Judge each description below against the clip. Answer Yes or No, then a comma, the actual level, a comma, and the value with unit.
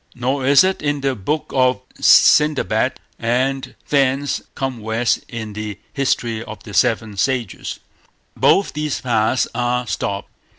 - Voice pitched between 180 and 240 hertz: No, low, 125 Hz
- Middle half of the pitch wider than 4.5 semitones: No, average, 3.7 semitones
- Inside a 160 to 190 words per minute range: No, slow, 135 wpm